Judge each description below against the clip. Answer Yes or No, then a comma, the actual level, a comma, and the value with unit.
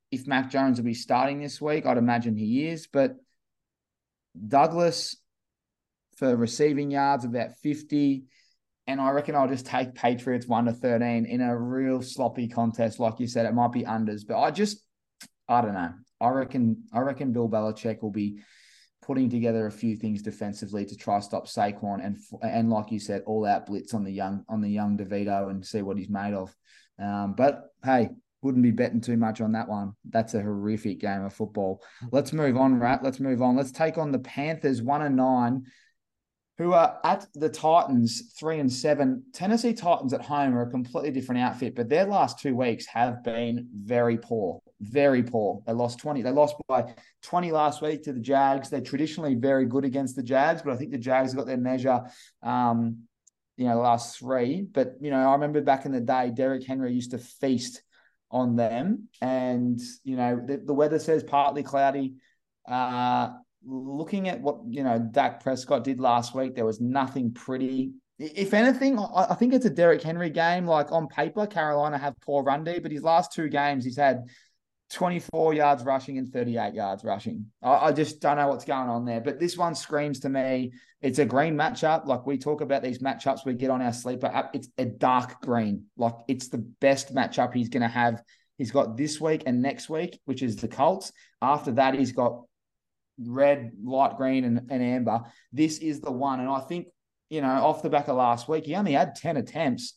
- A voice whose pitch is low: Yes, low, 130 Hz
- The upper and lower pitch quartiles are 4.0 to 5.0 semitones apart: No, average, 3.5 semitones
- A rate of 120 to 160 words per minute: No, average, 200 wpm